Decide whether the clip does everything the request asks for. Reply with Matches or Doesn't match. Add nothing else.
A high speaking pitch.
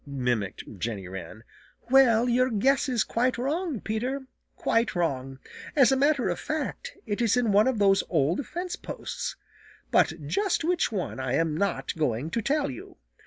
Matches